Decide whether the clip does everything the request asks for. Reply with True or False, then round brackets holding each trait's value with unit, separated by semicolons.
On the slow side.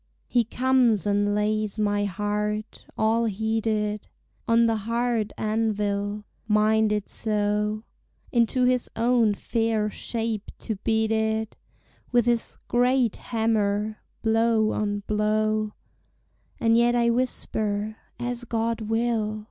True (110 wpm)